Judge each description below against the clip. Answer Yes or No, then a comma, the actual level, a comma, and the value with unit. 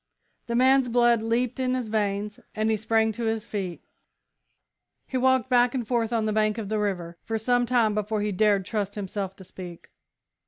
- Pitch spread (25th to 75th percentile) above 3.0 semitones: No, narrow, 2.6 semitones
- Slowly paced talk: No, average, 195 wpm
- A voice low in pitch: No, high, 220 Hz